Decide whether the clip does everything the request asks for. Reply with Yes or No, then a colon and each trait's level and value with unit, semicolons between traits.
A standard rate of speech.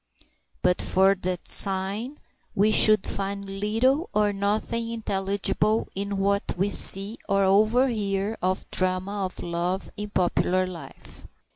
No: slow, 130 wpm